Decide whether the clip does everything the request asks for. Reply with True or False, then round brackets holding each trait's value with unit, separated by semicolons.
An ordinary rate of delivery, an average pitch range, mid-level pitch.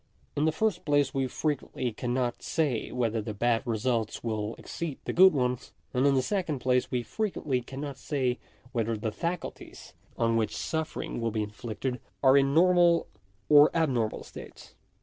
False (165 wpm; 4.6 semitones; 130 Hz)